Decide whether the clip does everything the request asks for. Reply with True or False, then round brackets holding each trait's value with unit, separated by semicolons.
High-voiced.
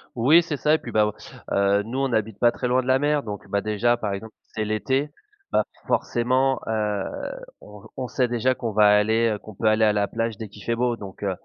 False (110 Hz)